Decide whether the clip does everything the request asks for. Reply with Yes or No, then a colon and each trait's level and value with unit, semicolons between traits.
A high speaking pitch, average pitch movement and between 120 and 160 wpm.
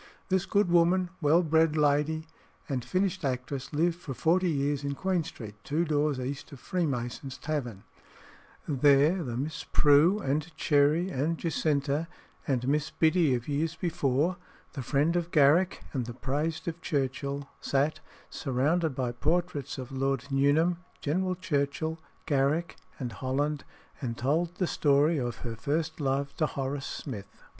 No: medium, 145 Hz; average, 3.3 semitones; average, 150 wpm